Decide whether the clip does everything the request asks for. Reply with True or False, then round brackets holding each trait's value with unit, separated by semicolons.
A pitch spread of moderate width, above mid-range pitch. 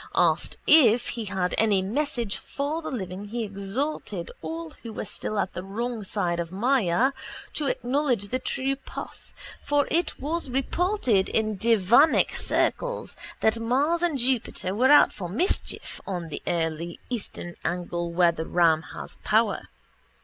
False (6.7 semitones; 220 Hz)